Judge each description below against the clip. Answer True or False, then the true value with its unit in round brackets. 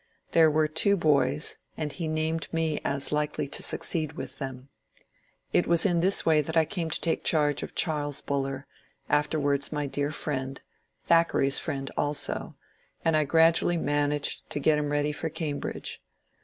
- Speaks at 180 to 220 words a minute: True (185 wpm)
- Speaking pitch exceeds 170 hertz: False (150 Hz)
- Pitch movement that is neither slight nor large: False (2.2 semitones)